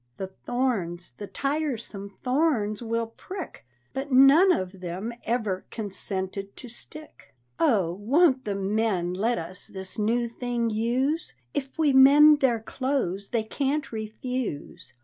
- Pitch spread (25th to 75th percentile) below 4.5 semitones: No, wide, 5.4 semitones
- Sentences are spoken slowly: Yes, slow, 130 wpm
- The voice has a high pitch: Yes, high, 230 Hz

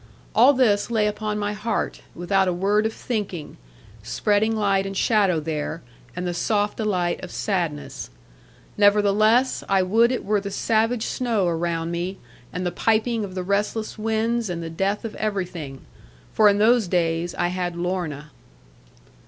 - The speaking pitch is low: No, high, 200 Hz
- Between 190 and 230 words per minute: No, average, 160 wpm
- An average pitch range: Yes, average, 3.6 semitones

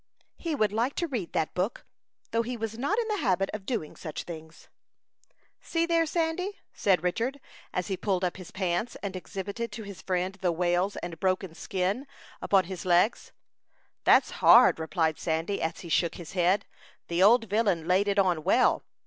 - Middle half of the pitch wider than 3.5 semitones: Yes, average, 4.5 semitones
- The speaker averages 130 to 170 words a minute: No, average, 185 wpm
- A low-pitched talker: No, high, 190 Hz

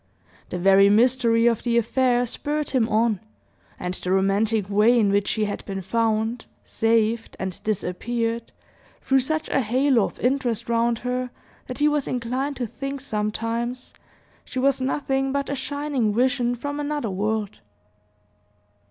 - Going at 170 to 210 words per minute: No, average, 150 wpm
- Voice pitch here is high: Yes, high, 235 Hz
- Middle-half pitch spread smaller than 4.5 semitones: Yes, average, 3.4 semitones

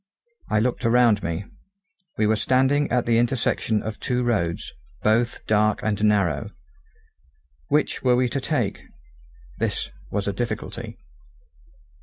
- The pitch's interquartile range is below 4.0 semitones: Yes, average, 2.9 semitones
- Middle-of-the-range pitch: No, low, 110 Hz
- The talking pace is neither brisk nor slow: No, slow, 130 wpm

